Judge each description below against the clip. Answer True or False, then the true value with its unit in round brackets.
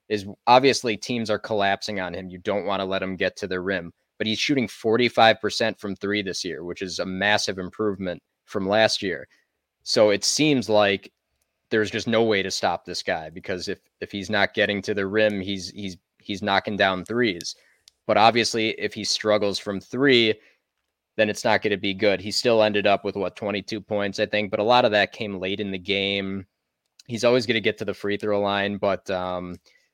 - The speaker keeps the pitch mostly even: True (2.0 semitones)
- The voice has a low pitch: True (100 Hz)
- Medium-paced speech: False (210 wpm)